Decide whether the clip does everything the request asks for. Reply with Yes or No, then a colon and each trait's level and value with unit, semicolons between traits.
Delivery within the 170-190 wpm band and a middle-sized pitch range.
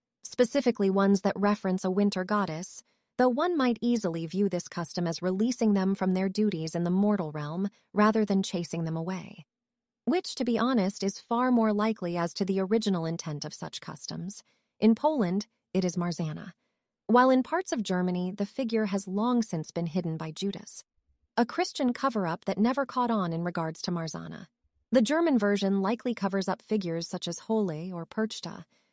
Yes: average, 180 wpm; average, 4.7 semitones